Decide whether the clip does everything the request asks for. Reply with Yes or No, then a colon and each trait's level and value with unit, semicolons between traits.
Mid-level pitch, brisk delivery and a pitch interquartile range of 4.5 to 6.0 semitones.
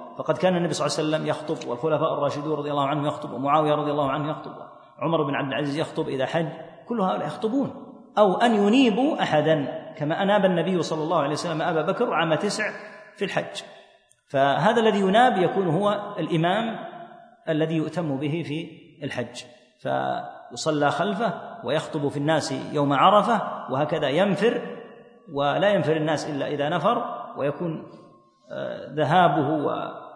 Yes: medium, 160 Hz; fast, 150 wpm; wide, 5.6 semitones